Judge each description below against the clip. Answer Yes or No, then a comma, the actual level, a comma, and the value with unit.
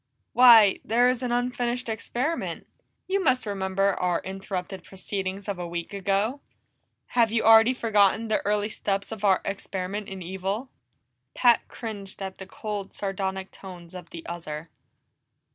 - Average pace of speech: Yes, average, 145 wpm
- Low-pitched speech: No, high, 200 Hz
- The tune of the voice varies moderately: Yes, average, 3.2 semitones